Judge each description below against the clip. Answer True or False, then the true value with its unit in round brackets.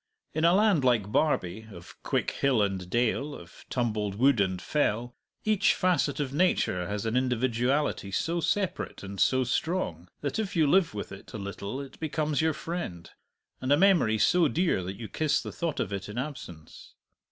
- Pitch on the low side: True (130 Hz)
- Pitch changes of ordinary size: False (7.5 semitones)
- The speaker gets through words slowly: False (185 wpm)